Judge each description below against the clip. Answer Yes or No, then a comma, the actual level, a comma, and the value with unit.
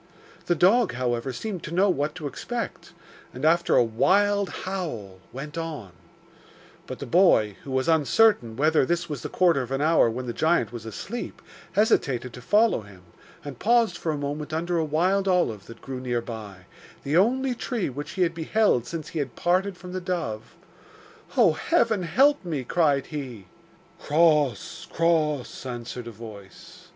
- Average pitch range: No, wide, 6.7 semitones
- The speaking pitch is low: No, medium, 155 Hz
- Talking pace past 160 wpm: Yes, average, 170 wpm